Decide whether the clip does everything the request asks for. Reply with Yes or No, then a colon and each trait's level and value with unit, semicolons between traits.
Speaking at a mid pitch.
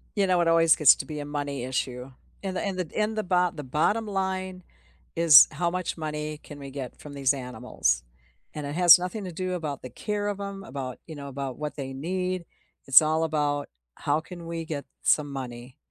Yes: medium, 155 Hz